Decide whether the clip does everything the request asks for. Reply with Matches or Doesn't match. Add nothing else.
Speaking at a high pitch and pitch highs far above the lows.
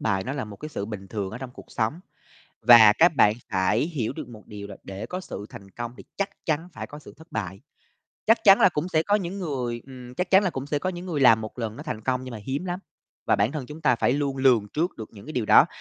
Doesn't match